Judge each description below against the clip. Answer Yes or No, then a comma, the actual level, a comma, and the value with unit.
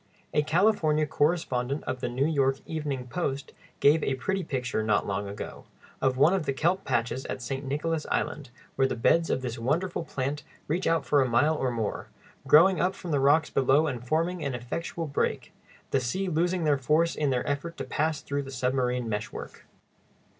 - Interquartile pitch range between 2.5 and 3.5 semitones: No, average, 4.0 semitones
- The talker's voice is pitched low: No, medium, 145 Hz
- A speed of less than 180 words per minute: No, average, 190 wpm